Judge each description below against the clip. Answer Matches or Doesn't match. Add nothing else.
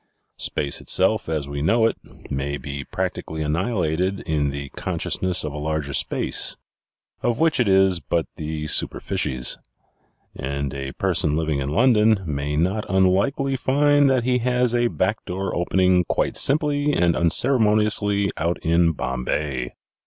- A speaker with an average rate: Matches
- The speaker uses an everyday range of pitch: Doesn't match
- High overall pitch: Doesn't match